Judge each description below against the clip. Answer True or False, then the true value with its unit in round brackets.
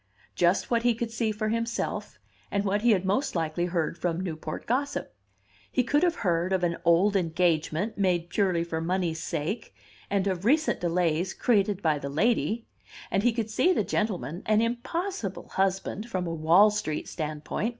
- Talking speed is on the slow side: False (175 wpm)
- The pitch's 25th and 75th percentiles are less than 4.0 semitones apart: False (4.9 semitones)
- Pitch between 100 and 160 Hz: False (190 Hz)